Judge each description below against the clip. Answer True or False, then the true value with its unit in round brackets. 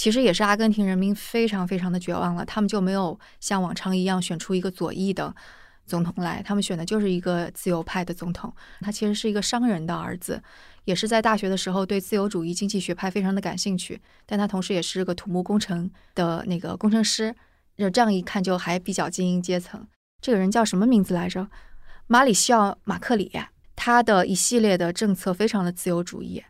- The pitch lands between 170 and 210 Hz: True (190 Hz)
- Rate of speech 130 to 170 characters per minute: False (330 characters per minute)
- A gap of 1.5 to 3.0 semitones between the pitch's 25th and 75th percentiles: True (2.5 semitones)